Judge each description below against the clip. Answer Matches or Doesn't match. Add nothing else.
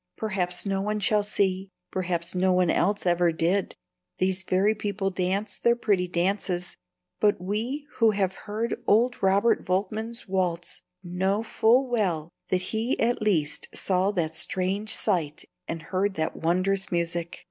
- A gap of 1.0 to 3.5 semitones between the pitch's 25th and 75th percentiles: Matches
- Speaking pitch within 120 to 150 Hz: Doesn't match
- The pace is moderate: Matches